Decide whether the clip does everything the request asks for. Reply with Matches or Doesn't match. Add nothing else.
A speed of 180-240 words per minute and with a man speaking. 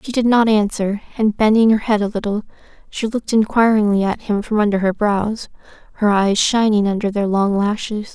Doesn't match